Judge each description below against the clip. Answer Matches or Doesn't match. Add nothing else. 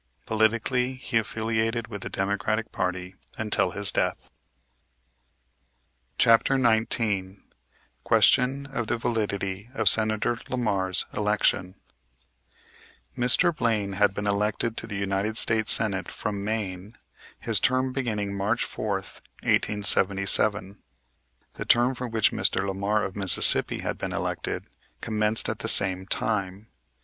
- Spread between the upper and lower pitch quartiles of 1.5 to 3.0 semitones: Matches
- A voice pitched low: Matches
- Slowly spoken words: Matches